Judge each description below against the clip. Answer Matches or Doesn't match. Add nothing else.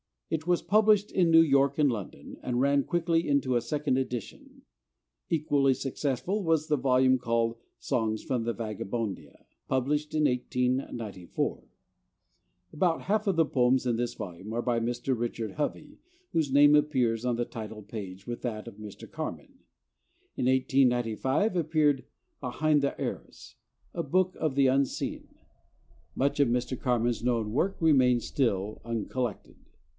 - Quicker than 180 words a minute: Doesn't match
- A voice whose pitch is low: Matches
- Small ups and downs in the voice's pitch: Doesn't match